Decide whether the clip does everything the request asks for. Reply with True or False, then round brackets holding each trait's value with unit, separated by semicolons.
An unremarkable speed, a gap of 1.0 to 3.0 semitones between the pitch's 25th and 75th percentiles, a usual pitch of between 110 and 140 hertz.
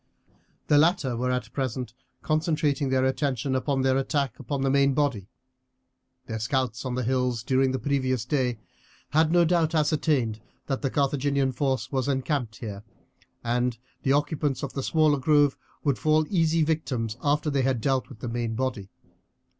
True (165 wpm; 2.7 semitones; 135 Hz)